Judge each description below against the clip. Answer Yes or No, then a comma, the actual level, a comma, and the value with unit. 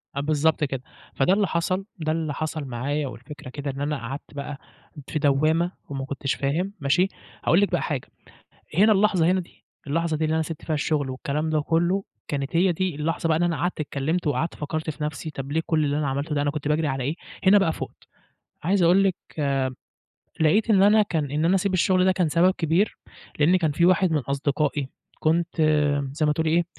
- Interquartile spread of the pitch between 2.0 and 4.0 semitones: Yes, average, 3.3 semitones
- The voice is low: No, medium, 155 Hz